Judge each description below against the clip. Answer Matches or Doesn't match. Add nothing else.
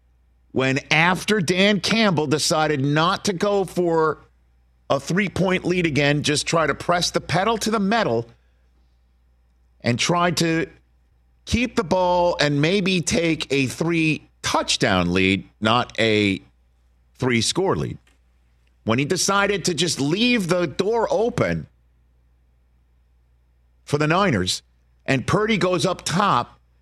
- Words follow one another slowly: Matches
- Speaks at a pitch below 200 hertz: Matches